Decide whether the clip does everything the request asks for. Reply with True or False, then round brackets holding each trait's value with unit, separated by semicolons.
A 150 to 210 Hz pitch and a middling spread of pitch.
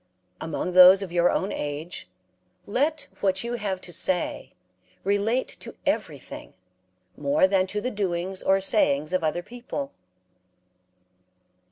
True (190 Hz; 3.1 semitones)